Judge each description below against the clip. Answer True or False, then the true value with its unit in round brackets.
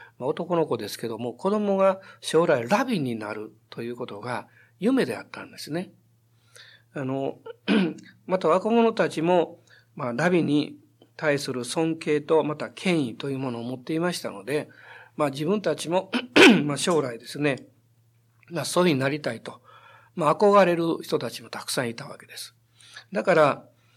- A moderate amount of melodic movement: False (6.6 semitones)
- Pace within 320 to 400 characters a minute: False (300 characters per minute)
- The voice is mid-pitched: True (150 Hz)